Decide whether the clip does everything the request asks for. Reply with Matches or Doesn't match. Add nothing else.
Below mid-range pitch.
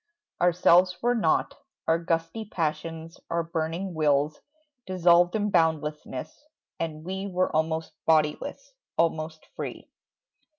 Doesn't match